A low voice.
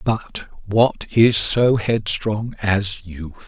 Yes: low, 105 Hz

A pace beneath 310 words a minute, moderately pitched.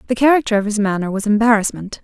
No: fast, 205 wpm; high, 215 Hz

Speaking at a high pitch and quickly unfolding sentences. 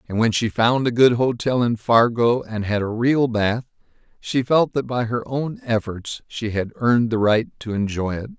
No: low, 115 Hz; fast, 210 wpm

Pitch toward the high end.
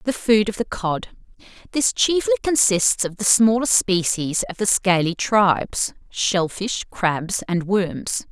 Yes: high, 200 Hz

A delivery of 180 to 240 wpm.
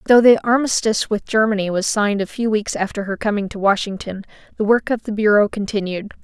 Yes: average, 200 wpm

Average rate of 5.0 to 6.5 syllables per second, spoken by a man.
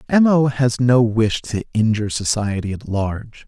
No: 4.6 syllables/s; male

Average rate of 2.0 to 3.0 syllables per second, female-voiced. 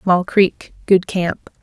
Yes: 2.9 syllables/s; female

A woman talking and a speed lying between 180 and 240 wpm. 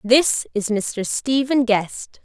No: female; slow, 135 wpm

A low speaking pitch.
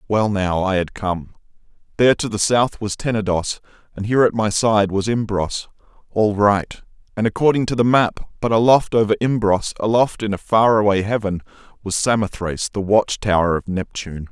Yes: low, 105 Hz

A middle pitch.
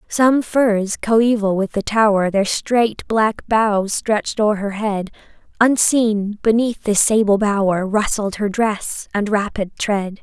No: high, 210 Hz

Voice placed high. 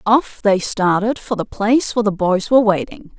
Yes: high, 210 Hz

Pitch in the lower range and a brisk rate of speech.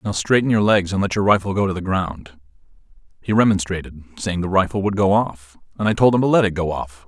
Yes: very low, 95 Hz; fast, 245 wpm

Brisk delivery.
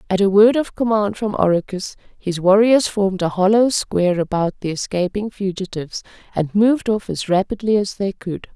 No: average, 175 wpm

